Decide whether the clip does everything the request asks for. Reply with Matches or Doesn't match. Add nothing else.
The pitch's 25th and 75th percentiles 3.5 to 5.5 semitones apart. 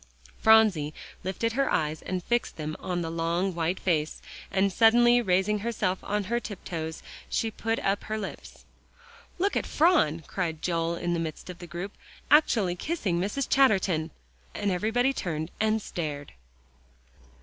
Matches